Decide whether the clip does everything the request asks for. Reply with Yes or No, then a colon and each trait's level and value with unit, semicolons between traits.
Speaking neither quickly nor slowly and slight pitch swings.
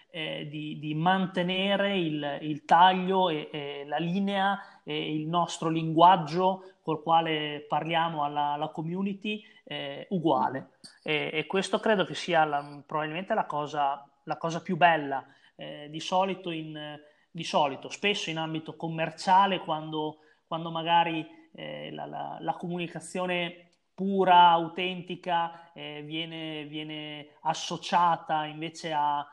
No: average, 130 wpm; average, 3.0 semitones